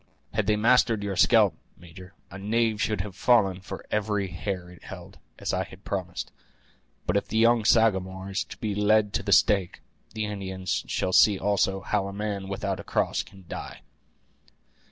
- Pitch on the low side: Yes, low, 100 Hz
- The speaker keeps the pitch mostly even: Yes, narrow, 2.2 semitones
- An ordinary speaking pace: Yes, average, 175 wpm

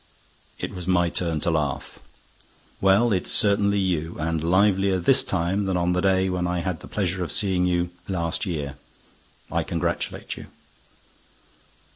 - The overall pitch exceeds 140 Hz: No, very low, 90 Hz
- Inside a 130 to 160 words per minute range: Yes, average, 150 wpm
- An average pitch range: No, narrow, 2.2 semitones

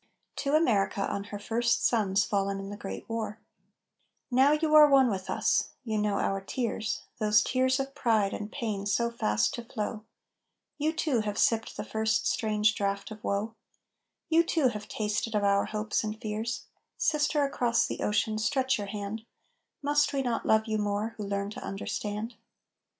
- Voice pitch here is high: Yes, high, 220 Hz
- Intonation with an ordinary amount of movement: Yes, average, 3.2 semitones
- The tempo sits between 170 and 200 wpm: Yes, average, 175 wpm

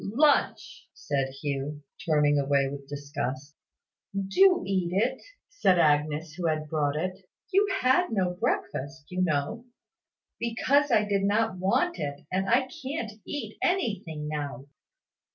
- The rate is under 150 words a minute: Yes, slow, 135 wpm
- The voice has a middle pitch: Yes, medium, 180 Hz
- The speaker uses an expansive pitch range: Yes, wide, 7.5 semitones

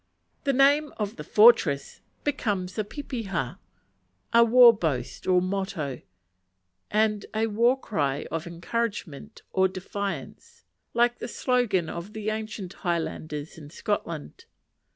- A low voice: No, high, 200 Hz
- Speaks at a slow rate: Yes, slow, 120 wpm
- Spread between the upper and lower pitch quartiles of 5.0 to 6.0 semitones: Yes, wide, 5.5 semitones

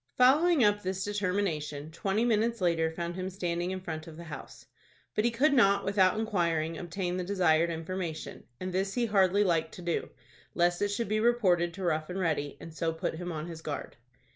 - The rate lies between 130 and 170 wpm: No, average, 200 wpm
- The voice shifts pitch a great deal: No, average, 3.7 semitones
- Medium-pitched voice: Yes, medium, 180 Hz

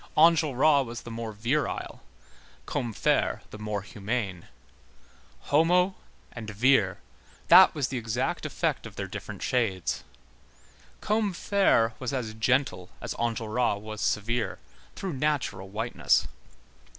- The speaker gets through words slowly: Yes, slow, 115 wpm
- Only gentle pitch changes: No, average, 4.8 semitones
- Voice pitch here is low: Yes, low, 120 Hz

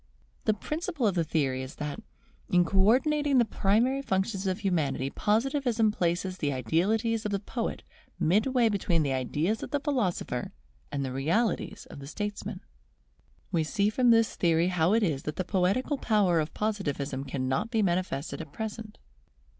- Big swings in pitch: Yes, wide, 6.1 semitones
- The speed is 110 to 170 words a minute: Yes, average, 165 wpm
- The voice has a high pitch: Yes, high, 195 Hz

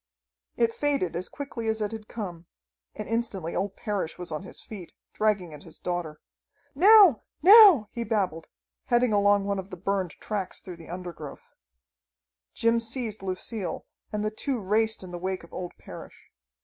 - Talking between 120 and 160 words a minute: No, average, 170 wpm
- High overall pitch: Yes, high, 205 Hz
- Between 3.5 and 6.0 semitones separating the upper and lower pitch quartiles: Yes, average, 4.1 semitones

